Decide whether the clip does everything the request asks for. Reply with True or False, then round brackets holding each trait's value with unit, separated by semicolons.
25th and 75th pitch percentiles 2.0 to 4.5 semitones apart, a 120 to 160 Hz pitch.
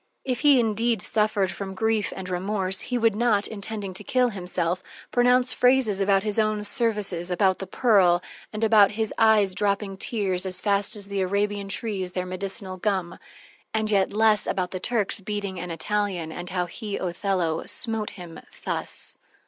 False (2.8 semitones; 200 Hz)